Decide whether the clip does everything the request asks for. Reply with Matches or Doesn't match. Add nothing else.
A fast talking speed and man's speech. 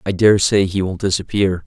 Doesn't match